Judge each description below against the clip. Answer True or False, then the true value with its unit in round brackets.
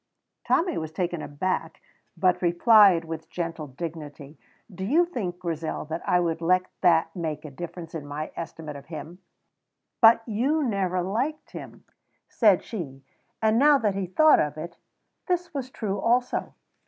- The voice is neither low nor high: True (180 Hz)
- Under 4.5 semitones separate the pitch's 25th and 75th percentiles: False (5.5 semitones)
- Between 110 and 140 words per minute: False (155 wpm)